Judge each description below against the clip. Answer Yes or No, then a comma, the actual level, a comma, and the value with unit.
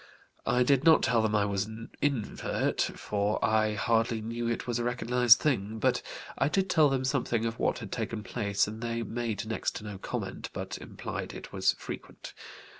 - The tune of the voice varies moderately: No, narrow, 2.3 semitones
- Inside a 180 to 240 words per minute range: Yes, average, 190 wpm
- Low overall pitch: Yes, low, 115 Hz